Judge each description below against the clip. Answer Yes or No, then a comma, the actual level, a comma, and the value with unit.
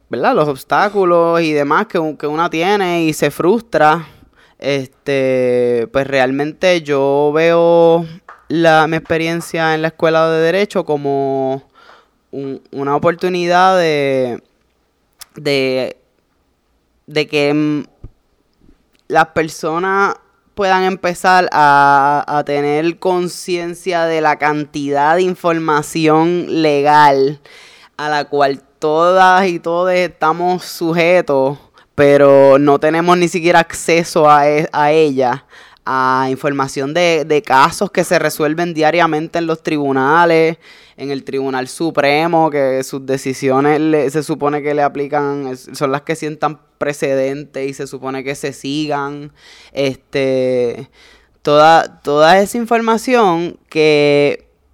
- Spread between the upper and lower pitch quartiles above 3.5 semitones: No, average, 3.2 semitones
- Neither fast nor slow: No, slow, 120 wpm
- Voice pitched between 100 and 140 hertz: No, medium, 150 Hz